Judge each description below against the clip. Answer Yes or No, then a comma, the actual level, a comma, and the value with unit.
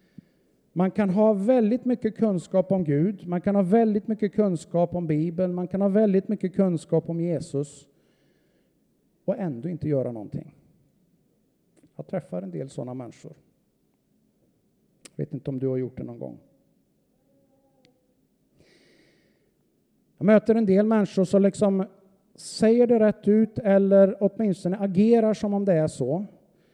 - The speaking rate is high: No, average, 145 wpm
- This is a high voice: Yes, high, 195 Hz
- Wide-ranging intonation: No, average, 4.5 semitones